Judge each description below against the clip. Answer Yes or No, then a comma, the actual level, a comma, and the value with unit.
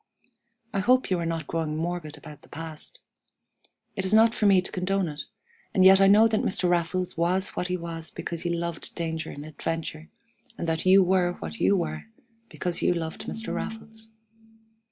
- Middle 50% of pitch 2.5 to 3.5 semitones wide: Yes, average, 2.9 semitones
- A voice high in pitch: No, medium, 175 Hz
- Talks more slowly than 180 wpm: No, average, 190 wpm